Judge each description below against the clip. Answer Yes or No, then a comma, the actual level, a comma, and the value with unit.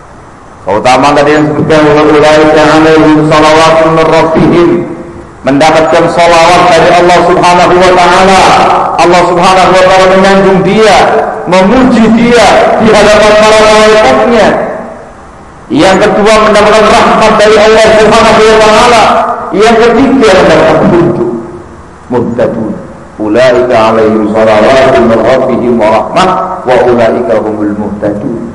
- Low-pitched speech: No, medium, 175 Hz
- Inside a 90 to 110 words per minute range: Yes, average, 105 wpm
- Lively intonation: Yes, wide, 5.8 semitones